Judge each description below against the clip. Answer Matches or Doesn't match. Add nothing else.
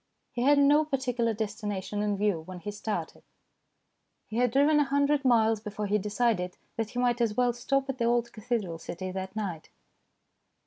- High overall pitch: Matches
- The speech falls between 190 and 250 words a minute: Doesn't match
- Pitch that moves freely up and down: Doesn't match